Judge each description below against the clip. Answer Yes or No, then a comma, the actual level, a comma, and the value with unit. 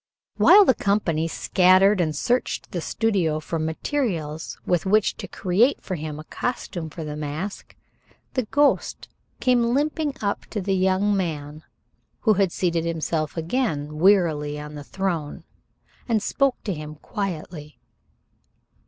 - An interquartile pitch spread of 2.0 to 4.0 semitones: No, average, 5.2 semitones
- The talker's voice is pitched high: No, medium, 180 Hz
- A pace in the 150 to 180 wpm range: No, average, 140 wpm